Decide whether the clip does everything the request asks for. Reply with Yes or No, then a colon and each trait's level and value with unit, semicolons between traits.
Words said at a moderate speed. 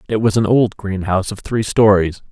No: fast, 235 wpm